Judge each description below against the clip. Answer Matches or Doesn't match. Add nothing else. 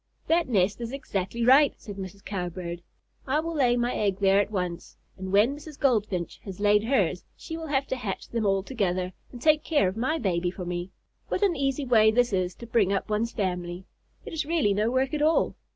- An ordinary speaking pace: Doesn't match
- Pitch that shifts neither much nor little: Doesn't match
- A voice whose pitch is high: Matches